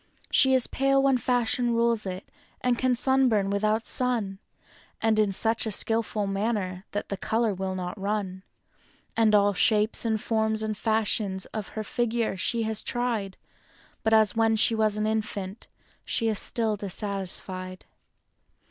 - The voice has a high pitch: Yes, high, 215 Hz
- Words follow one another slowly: No, average, 150 wpm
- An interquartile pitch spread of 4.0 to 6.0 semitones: No, narrow, 2.4 semitones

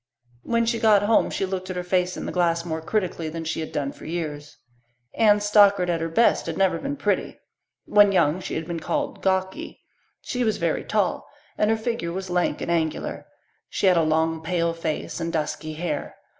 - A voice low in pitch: No, medium, 180 Hz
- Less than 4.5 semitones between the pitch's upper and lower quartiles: Yes, average, 3.9 semitones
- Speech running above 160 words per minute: Yes, fast, 205 wpm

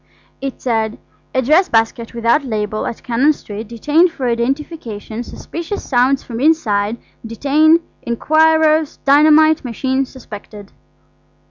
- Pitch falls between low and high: No, very high, 260 Hz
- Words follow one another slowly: Yes, slow, 115 wpm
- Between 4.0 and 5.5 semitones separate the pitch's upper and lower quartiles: Yes, average, 5.2 semitones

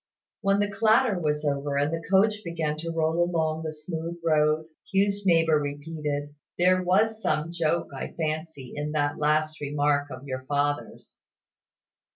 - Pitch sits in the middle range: Yes, medium, 155 Hz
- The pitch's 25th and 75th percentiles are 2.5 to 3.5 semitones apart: Yes, average, 2.9 semitones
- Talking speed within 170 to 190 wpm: No, average, 155 wpm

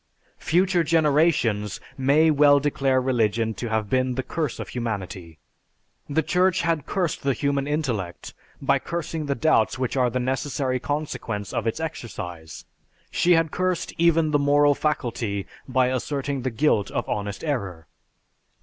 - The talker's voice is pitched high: No, low, 135 Hz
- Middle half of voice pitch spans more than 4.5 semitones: Yes, average, 5.2 semitones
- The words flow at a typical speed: Yes, average, 150 wpm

